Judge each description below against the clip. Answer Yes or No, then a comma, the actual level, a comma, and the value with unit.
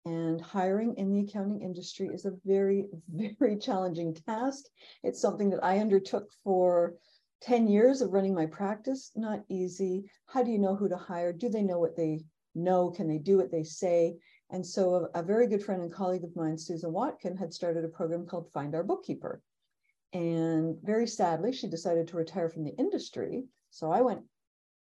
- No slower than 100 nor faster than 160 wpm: No, average, 190 wpm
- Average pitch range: Yes, average, 3.5 semitones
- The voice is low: No, medium, 185 Hz